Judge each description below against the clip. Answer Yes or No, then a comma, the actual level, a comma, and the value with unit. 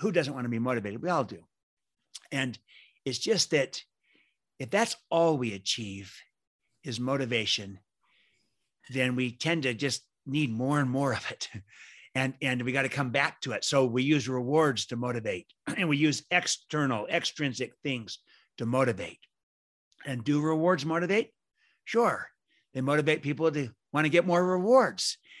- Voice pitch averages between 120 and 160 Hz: Yes, low, 135 Hz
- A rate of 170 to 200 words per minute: No, average, 160 wpm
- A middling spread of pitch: Yes, average, 4.4 semitones